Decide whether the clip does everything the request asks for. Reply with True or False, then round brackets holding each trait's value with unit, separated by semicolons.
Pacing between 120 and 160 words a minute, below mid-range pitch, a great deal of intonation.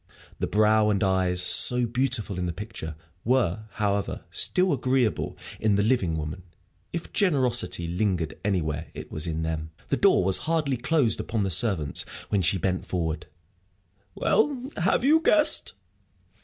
True (150 wpm; 105 Hz; 6.4 semitones)